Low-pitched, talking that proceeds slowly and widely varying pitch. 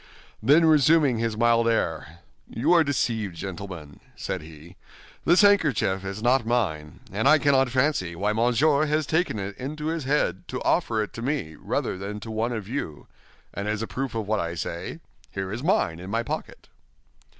No: low, 115 Hz; average, 185 wpm; wide, 6.6 semitones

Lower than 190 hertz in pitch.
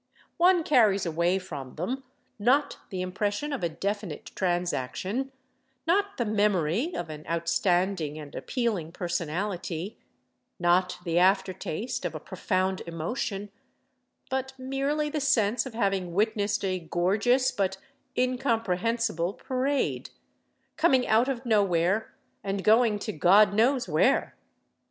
No: high, 205 Hz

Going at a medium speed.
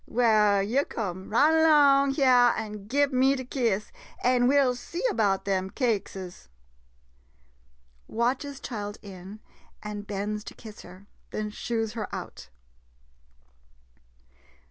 No: slow, 120 wpm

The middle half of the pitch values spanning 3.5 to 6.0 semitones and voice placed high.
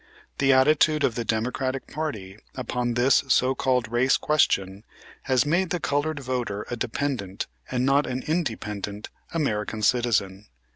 No: average, 4.4 semitones; low, 125 Hz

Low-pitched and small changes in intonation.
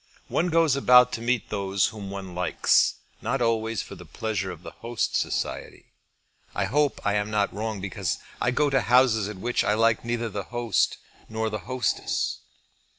No: low, 110 Hz; average, 3.2 semitones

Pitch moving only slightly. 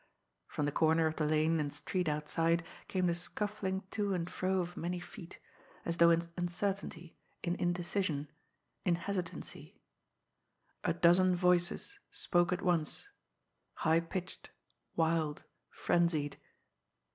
Yes: narrow, 1.9 semitones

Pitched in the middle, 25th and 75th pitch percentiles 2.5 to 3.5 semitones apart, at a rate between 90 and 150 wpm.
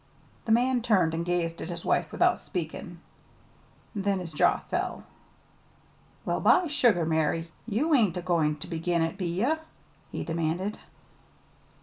No: medium, 175 Hz; average, 4.2 semitones; average, 145 wpm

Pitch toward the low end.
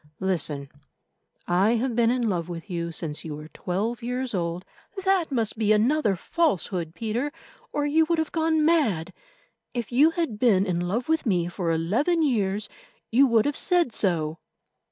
No: high, 220 Hz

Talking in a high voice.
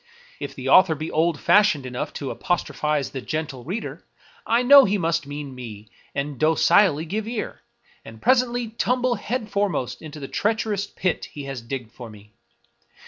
No: medium, 160 Hz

